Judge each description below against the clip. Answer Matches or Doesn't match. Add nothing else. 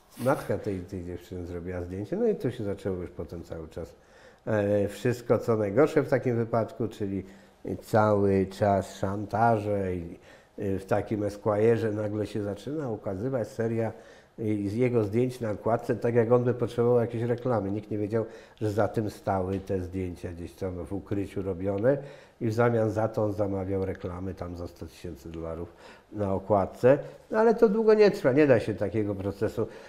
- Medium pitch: Doesn't match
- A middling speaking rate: Matches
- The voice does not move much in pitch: Doesn't match